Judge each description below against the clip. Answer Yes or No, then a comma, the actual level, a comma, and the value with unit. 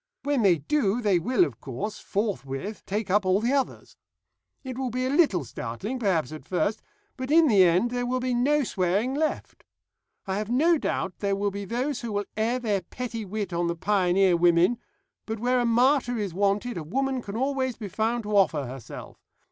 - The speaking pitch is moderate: No, high, 215 Hz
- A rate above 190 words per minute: Yes, average, 200 wpm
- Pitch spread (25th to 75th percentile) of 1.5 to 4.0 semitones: No, average, 5.1 semitones